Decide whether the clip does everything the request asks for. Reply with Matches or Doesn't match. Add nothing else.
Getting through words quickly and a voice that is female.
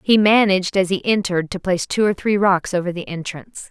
Matches